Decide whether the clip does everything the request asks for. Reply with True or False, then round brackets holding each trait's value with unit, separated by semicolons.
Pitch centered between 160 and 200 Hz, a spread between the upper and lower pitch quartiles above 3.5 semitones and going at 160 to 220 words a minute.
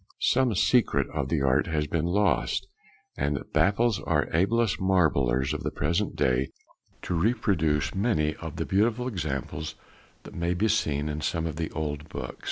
False (80 Hz; 5.6 semitones; 170 wpm)